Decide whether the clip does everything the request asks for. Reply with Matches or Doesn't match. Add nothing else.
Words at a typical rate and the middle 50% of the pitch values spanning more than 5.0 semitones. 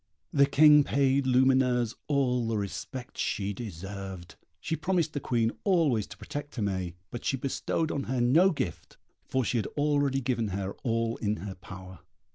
Matches